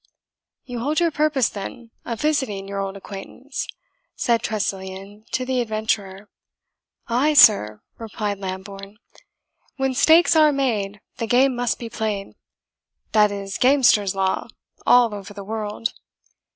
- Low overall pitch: No, high, 220 Hz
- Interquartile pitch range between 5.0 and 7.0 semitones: No, average, 4.3 semitones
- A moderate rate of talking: No, slow, 130 wpm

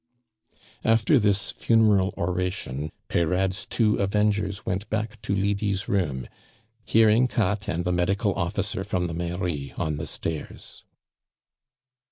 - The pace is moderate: No, slow, 120 wpm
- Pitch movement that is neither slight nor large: Yes, average, 3.2 semitones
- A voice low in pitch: Yes, very low, 95 Hz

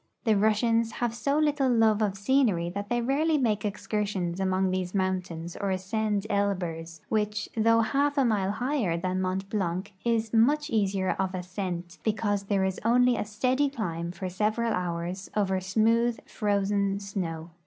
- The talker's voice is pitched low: No, high, 205 Hz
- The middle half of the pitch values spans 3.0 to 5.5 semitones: Yes, average, 3.4 semitones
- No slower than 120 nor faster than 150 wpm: No, average, 160 wpm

